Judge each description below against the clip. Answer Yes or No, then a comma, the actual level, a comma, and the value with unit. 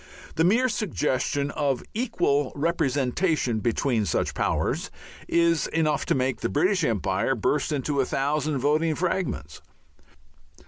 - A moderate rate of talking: No, slow, 125 wpm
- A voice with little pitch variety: No, average, 4.1 semitones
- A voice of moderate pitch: Yes, medium, 145 Hz